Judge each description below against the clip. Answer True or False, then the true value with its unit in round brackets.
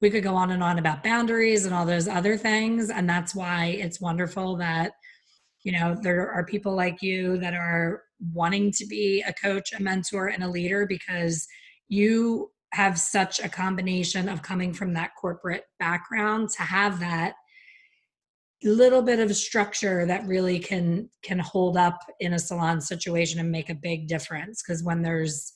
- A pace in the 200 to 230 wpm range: False (175 wpm)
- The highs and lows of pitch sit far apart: False (2.9 semitones)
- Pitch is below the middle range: False (185 Hz)